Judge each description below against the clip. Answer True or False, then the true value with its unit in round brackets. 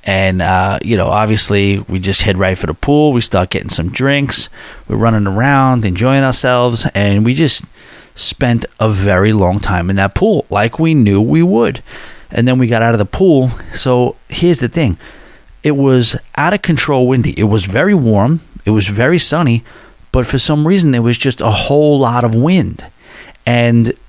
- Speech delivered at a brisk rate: False (190 wpm)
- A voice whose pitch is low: True (120 Hz)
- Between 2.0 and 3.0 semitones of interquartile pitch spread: False (4.9 semitones)